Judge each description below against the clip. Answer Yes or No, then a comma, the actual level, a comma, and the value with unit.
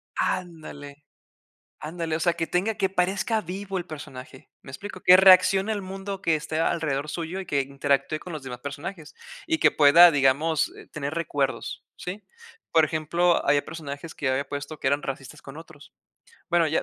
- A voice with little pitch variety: No, average, 4.1 semitones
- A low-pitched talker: No, medium, 160 Hz